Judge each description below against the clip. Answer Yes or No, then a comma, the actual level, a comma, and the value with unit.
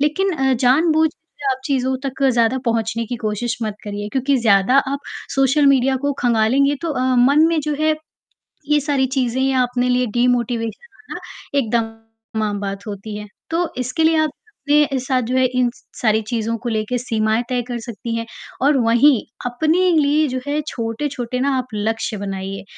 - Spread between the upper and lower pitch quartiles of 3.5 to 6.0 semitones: Yes, average, 3.8 semitones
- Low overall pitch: No, very high, 250 Hz